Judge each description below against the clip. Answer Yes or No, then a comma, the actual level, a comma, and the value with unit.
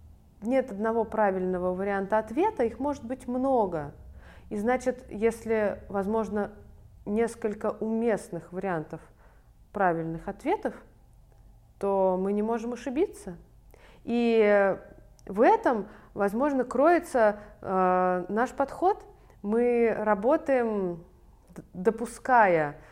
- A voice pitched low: No, high, 220 Hz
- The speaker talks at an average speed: No, slow, 90 wpm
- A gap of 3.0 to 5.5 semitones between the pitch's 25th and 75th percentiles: Yes, average, 4.3 semitones